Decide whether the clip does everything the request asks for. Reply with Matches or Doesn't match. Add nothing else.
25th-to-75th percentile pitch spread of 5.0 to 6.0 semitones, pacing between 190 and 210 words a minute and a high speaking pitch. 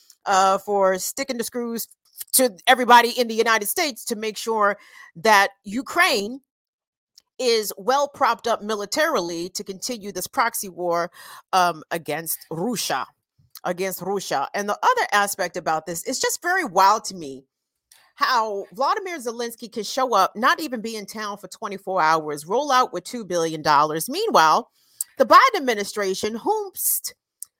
Doesn't match